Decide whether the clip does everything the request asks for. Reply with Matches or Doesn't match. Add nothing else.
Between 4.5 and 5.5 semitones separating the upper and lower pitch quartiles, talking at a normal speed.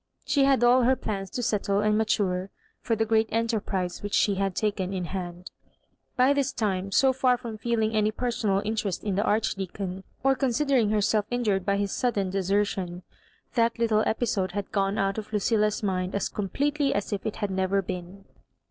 Doesn't match